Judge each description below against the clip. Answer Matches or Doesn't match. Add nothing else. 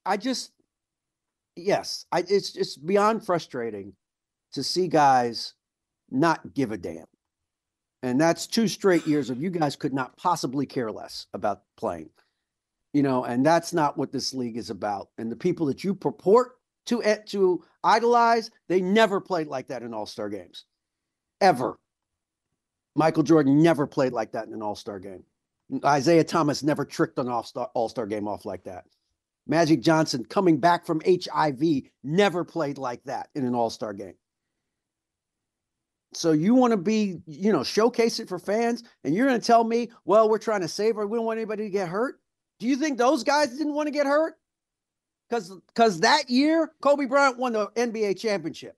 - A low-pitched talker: Doesn't match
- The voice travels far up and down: Matches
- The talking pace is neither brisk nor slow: Matches